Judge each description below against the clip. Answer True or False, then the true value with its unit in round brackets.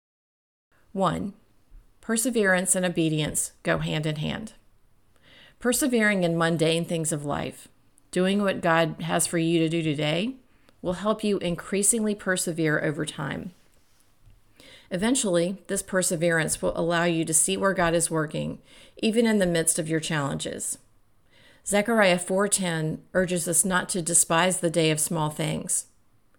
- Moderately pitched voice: True (170 Hz)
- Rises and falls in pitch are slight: False (3.3 semitones)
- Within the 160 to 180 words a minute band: False (140 wpm)